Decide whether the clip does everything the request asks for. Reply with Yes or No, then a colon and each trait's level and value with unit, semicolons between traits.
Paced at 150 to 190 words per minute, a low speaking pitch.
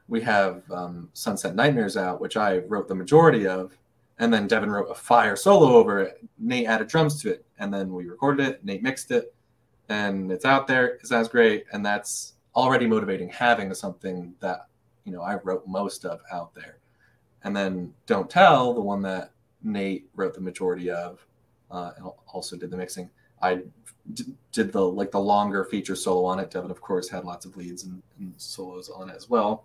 No: average, 200 wpm; low, 100 Hz